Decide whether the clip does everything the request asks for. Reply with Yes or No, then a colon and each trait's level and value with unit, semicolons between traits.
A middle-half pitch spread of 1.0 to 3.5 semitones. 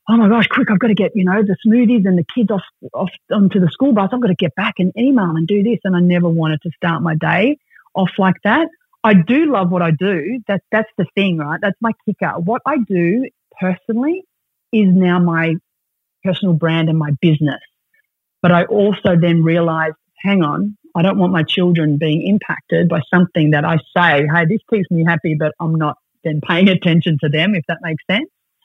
No: average, 4.2 semitones